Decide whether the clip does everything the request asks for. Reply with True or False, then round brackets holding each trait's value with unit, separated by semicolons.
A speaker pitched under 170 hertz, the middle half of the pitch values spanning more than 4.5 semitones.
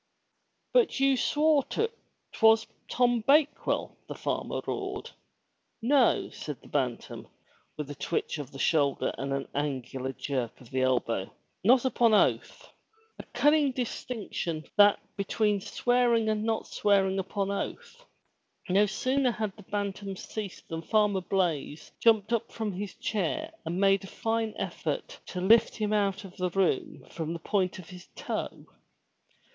False (200 Hz; 5.3 semitones)